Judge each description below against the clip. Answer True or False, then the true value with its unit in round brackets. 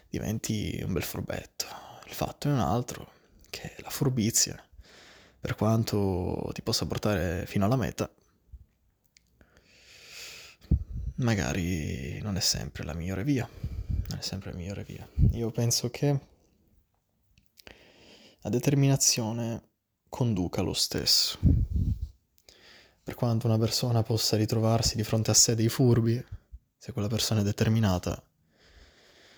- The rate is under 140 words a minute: True (120 wpm)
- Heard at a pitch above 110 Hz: False (105 Hz)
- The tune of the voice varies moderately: True (3.7 semitones)